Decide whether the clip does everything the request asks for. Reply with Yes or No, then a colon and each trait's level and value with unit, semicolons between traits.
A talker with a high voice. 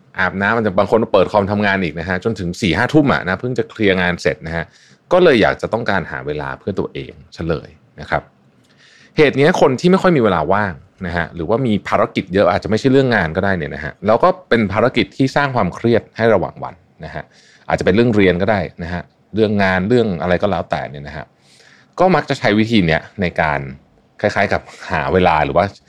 No: very low, 95 Hz